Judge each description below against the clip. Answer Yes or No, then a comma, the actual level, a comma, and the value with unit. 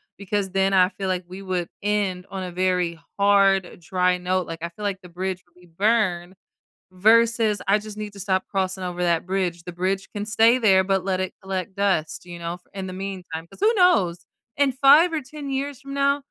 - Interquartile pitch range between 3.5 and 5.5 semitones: No, narrow, 2.6 semitones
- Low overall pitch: No, high, 190 Hz